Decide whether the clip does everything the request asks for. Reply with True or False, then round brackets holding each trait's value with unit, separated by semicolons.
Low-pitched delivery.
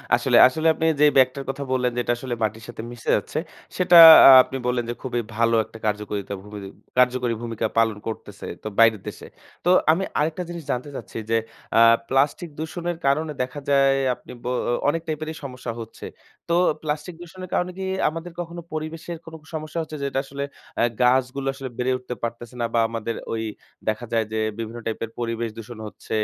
True (130 Hz)